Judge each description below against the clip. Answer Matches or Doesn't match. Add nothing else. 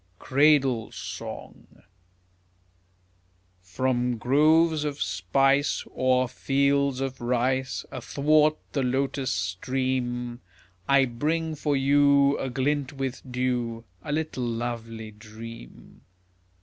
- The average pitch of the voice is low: Matches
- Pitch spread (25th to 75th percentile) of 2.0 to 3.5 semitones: Matches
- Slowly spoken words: Matches